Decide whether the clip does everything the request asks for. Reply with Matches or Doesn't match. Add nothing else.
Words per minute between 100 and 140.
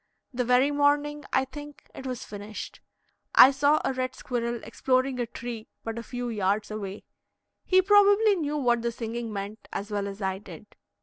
Doesn't match